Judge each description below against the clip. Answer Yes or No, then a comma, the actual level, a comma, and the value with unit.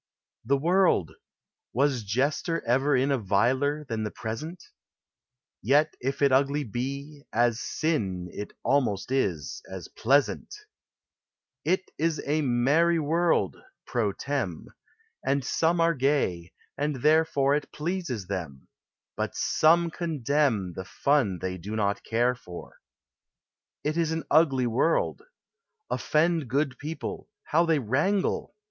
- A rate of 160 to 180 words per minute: No, slow, 135 wpm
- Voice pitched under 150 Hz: Yes, medium, 140 Hz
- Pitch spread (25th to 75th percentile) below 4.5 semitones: No, average, 5.2 semitones